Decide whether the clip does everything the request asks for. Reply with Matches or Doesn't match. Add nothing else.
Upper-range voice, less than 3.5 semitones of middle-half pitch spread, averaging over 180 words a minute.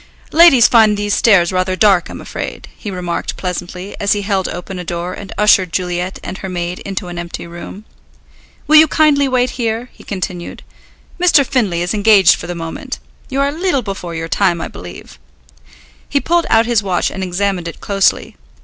Doesn't match